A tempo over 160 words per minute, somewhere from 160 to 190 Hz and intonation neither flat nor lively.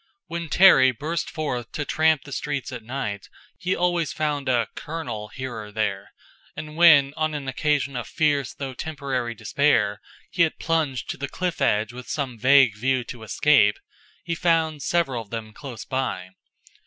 No: average, 170 wpm; low, 135 Hz; average, 4.6 semitones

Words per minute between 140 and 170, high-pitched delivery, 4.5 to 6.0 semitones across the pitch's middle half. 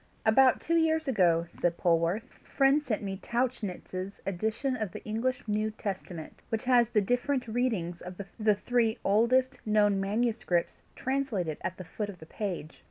Yes: average, 165 wpm; high, 215 Hz; average, 4.9 semitones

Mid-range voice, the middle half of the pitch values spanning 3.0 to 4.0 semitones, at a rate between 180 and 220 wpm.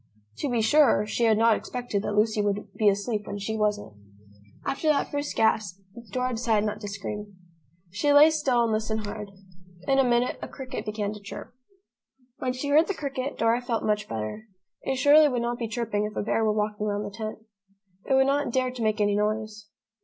No: high, 220 Hz; average, 3.4 semitones; fast, 205 wpm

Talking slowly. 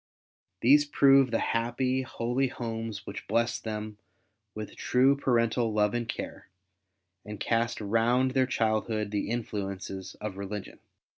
Yes: slow, 130 wpm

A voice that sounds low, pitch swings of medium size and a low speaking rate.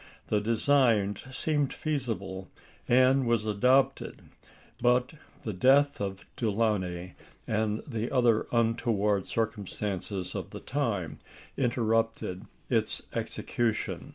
Yes: low, 115 Hz; average, 3.6 semitones; slow, 100 wpm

